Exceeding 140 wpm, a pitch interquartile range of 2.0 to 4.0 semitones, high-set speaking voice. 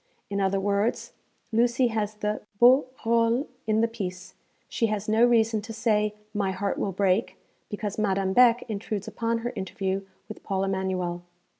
Yes: average, 160 wpm; average, 2.8 semitones; high, 210 Hz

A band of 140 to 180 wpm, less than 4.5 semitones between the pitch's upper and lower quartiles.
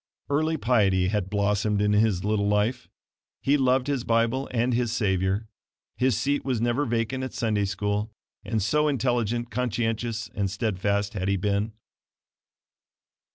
Yes: average, 145 wpm; average, 3.4 semitones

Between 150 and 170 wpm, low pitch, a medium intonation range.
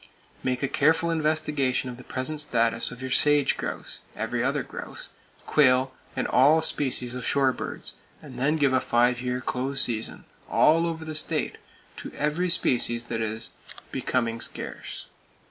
Yes: average, 155 wpm; low, 130 Hz; average, 3.4 semitones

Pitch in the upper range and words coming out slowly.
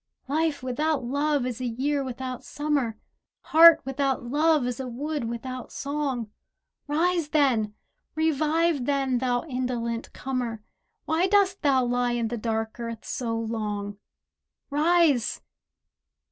Yes: very high, 260 Hz; slow, 125 wpm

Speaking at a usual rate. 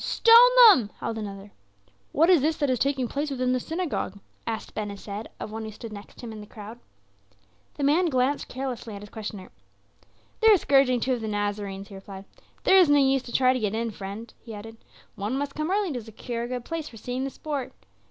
No: fast, 220 wpm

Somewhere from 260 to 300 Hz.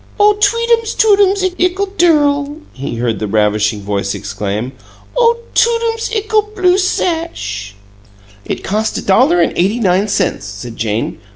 Yes: very high, 285 Hz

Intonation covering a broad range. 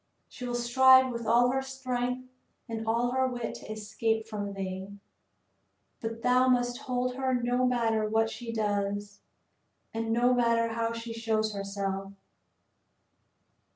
No: narrow, 2.4 semitones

